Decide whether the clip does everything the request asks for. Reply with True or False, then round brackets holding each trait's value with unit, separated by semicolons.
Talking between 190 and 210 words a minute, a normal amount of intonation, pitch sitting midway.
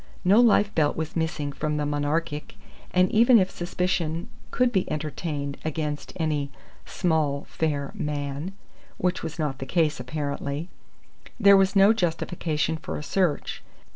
False (140 wpm; 3.6 semitones; 160 Hz)